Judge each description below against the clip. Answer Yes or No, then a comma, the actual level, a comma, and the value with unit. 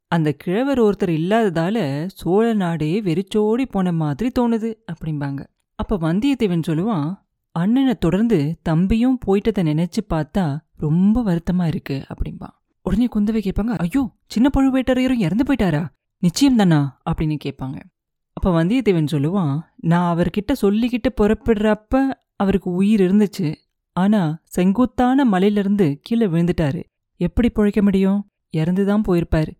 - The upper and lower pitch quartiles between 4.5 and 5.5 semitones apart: Yes, average, 5.2 semitones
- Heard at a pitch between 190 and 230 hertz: Yes, high, 195 Hz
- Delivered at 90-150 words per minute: Yes, average, 115 wpm